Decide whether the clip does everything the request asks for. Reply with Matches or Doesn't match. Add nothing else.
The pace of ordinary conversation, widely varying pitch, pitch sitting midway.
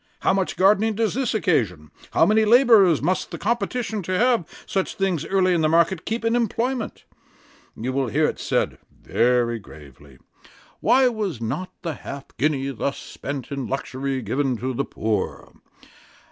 Matches